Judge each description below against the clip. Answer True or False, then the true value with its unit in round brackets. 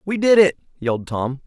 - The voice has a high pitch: False (160 Hz)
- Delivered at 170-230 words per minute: True (205 wpm)